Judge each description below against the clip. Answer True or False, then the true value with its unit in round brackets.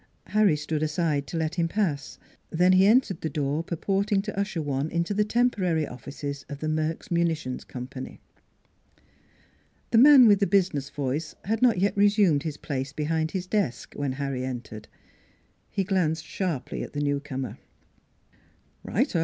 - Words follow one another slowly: False (160 wpm)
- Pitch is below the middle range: False (160 Hz)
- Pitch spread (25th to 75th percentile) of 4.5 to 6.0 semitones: True (5.6 semitones)